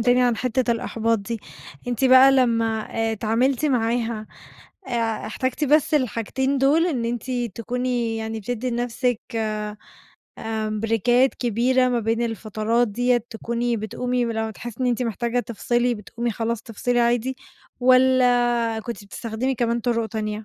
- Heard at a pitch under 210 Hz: No, high, 235 Hz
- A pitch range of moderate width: No, narrow, 1.8 semitones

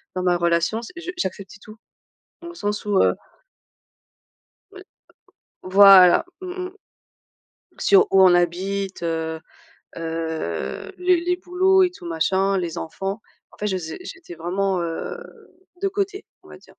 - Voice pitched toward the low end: No, high, 195 Hz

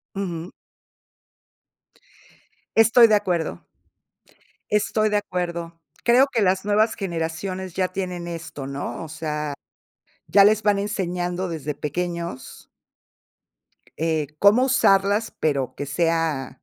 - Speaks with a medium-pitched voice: Yes, medium, 180 Hz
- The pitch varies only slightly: No, average, 3.9 semitones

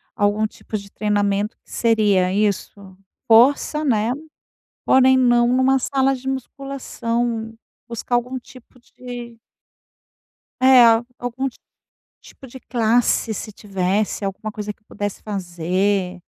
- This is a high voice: Yes, high, 225 Hz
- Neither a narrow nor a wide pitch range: Yes, average, 3.5 semitones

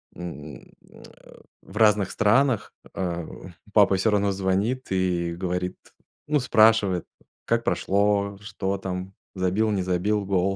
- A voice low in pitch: Yes, very low, 95 Hz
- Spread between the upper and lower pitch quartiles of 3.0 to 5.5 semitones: No, narrow, 2.4 semitones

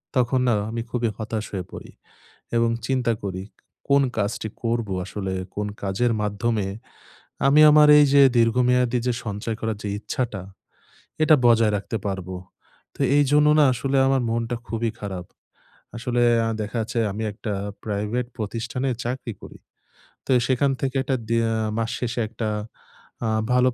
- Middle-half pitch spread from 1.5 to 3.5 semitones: Yes, average, 3.0 semitones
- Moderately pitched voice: No, low, 115 Hz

